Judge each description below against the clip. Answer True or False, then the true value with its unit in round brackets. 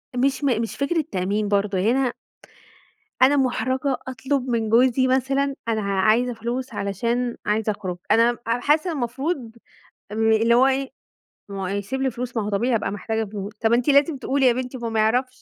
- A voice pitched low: False (240 Hz)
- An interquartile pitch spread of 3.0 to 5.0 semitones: True (3.4 semitones)